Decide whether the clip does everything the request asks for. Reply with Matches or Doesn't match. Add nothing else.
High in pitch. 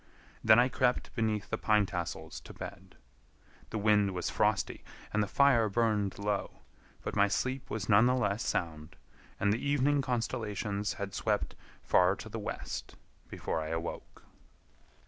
Doesn't match